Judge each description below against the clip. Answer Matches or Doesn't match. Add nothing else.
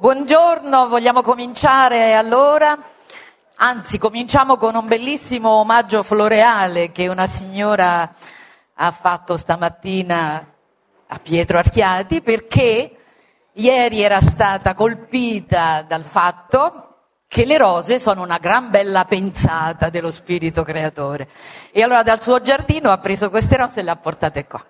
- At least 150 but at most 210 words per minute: Doesn't match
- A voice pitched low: Doesn't match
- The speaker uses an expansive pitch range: Matches